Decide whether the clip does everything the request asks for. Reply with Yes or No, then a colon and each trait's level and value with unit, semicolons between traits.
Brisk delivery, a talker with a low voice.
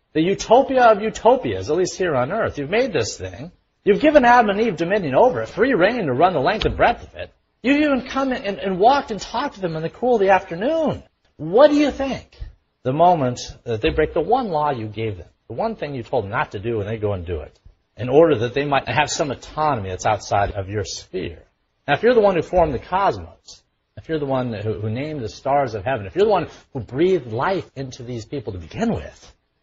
No: fast, 250 wpm; medium, 150 Hz